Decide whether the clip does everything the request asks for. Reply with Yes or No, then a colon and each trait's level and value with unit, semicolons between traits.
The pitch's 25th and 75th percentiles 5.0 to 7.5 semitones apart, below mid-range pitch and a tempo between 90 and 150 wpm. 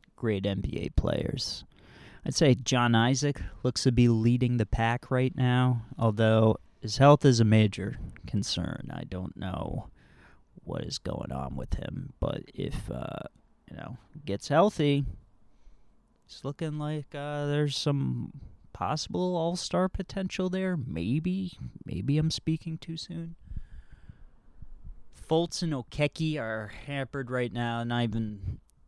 Yes: wide, 5.4 semitones; low, 125 Hz; slow, 135 wpm